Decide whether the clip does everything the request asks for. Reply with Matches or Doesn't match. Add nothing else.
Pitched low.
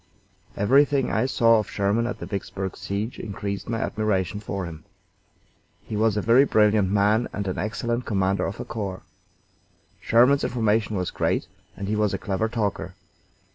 Matches